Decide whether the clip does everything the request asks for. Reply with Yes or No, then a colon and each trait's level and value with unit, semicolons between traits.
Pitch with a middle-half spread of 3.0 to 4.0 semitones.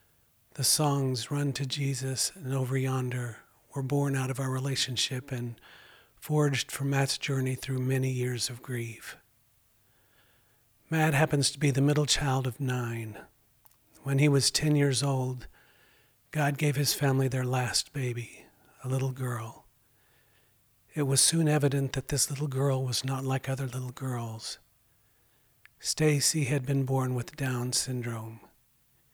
No: narrow, 2.4 semitones